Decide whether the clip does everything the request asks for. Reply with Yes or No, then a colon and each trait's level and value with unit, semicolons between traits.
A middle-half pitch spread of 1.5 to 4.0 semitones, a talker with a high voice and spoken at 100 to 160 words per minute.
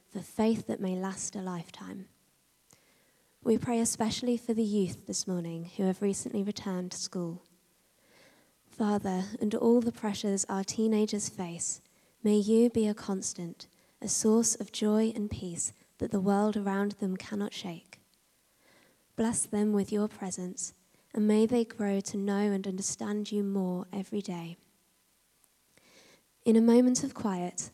Yes: average, 2.7 semitones; high, 205 Hz; average, 150 wpm